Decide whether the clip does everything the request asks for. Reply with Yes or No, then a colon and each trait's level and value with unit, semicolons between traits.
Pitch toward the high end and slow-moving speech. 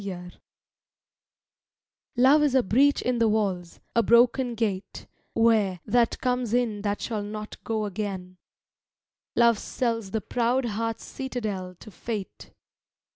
Yes: high, 225 Hz; slow, 130 wpm